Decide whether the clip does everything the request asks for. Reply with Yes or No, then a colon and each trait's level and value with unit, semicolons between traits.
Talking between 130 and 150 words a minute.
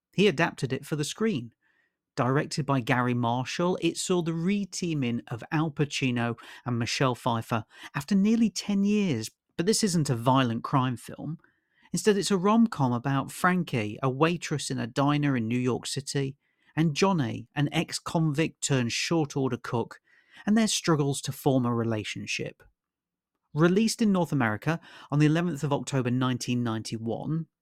No: average, 160 wpm